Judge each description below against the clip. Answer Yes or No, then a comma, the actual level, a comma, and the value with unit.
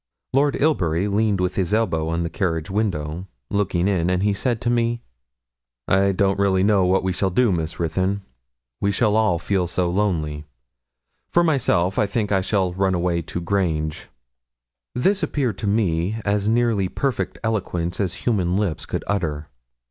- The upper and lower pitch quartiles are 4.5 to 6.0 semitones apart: No, average, 3.4 semitones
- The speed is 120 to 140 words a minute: No, average, 170 wpm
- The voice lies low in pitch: Yes, very low, 95 Hz